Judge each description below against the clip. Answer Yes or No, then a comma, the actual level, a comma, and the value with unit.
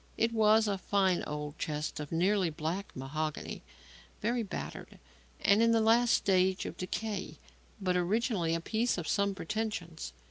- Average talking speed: Yes, average, 150 wpm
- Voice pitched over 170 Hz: Yes, high, 190 Hz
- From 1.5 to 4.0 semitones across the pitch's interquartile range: No, average, 5.0 semitones